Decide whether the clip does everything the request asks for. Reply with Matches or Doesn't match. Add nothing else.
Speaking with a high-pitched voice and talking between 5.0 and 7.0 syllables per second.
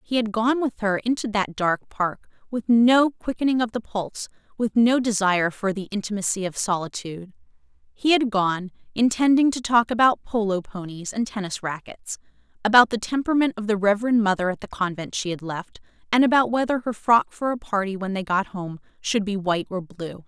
Matches